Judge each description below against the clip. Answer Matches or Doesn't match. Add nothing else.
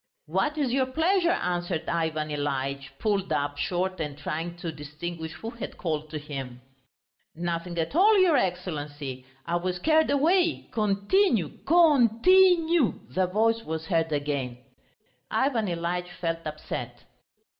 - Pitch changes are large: Matches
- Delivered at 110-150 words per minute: Matches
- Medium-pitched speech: Matches